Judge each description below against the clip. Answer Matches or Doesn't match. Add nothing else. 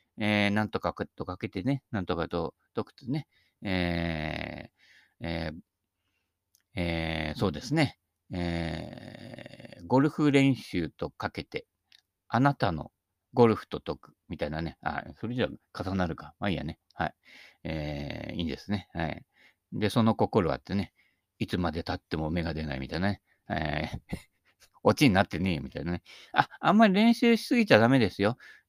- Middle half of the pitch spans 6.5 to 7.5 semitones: Doesn't match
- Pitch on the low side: Matches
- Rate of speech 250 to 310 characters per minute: Matches